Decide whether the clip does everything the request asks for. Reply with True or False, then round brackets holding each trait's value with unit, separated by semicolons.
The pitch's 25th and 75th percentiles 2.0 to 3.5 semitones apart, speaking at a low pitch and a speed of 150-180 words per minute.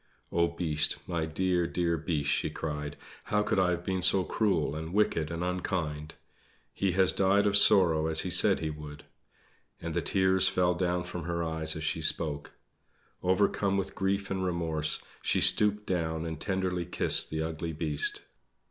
True (2.9 semitones; 85 Hz; 175 wpm)